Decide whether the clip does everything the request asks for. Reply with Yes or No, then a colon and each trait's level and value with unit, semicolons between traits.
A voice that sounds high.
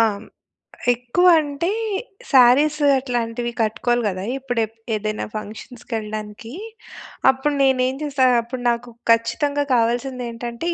Yes: high, 245 Hz